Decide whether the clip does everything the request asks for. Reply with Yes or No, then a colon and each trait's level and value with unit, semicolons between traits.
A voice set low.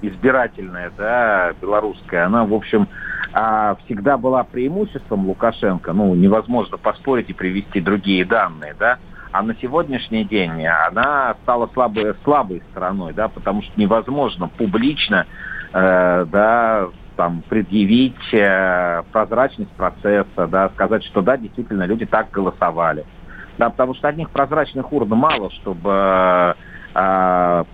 Yes: low, 105 Hz